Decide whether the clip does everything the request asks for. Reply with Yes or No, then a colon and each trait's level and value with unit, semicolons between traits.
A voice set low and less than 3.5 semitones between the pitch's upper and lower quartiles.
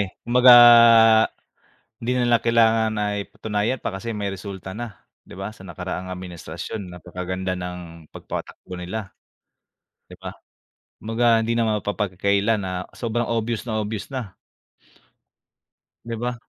No: low, 105 Hz; average, 3.8 semitones